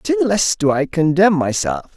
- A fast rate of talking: No, average, 185 wpm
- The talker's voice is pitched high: No, medium, 170 Hz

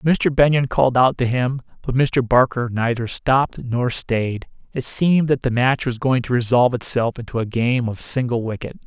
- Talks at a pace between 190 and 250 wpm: Yes, average, 195 wpm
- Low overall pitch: Yes, low, 125 Hz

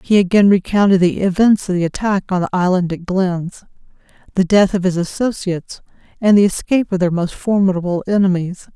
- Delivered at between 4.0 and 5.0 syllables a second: No, 5.6 syllables/s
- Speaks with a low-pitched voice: No, high, 190 Hz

